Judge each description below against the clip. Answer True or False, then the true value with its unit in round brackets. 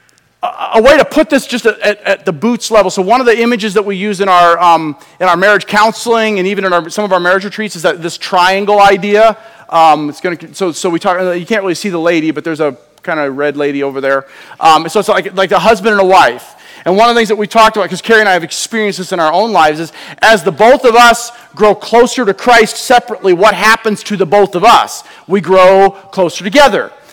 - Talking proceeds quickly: True (255 wpm)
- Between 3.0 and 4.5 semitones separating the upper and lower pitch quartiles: True (3.8 semitones)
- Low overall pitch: False (195 Hz)